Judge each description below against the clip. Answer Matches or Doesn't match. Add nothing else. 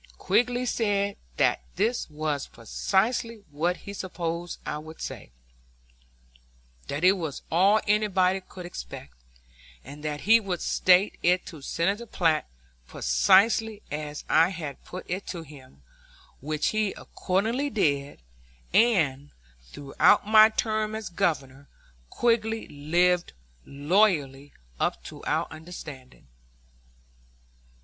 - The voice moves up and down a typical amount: Doesn't match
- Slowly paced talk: Matches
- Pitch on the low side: Doesn't match